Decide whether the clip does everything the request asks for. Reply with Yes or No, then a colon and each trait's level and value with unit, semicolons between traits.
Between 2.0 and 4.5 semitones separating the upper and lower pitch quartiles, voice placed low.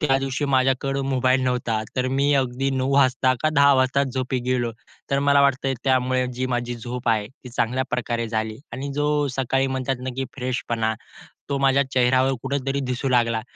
No: narrow, 1.6 semitones; low, 130 Hz